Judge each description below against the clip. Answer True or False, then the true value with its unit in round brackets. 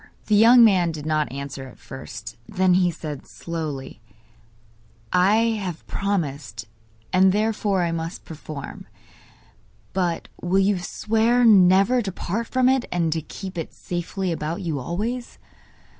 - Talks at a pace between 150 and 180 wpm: False (140 wpm)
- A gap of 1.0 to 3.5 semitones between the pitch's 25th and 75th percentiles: False (4.7 semitones)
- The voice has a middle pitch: True (180 Hz)